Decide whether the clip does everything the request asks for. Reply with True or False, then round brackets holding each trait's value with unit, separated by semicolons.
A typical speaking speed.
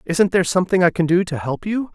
False (275 wpm)